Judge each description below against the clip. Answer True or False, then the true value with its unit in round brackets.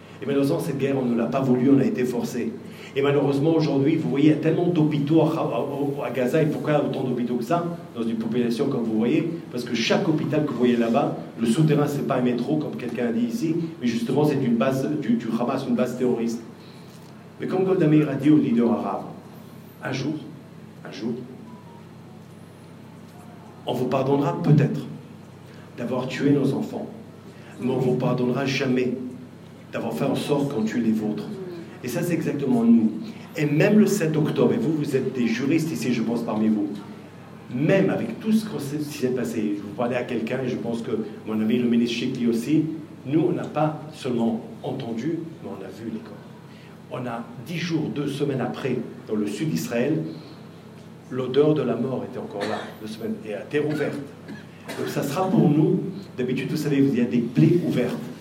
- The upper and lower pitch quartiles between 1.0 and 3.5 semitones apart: False (4.3 semitones)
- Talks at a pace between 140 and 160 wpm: False (205 wpm)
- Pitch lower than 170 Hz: True (140 Hz)